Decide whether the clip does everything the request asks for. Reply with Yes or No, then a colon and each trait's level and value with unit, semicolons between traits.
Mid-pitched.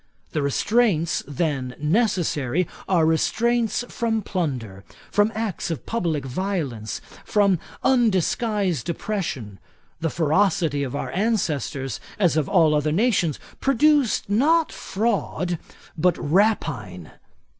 Yes: medium, 175 Hz